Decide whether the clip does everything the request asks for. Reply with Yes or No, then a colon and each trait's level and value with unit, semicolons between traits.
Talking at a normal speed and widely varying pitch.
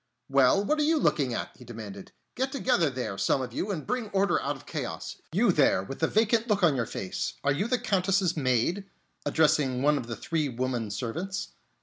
No: fast, 210 wpm; wide, 8.1 semitones